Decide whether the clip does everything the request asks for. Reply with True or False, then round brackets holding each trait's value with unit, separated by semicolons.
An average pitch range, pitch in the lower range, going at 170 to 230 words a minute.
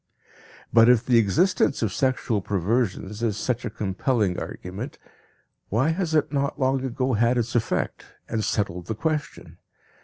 False (4.2 semitones; 115 Hz; 150 wpm)